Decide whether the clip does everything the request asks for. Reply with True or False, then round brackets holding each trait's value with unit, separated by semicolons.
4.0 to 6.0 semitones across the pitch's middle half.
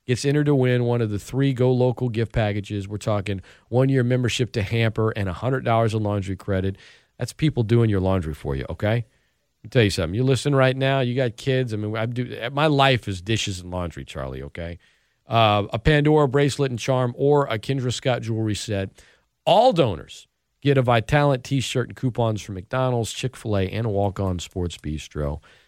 True (4.4 semitones)